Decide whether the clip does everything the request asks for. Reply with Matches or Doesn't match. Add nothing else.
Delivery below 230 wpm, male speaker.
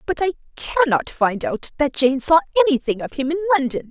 Doesn't match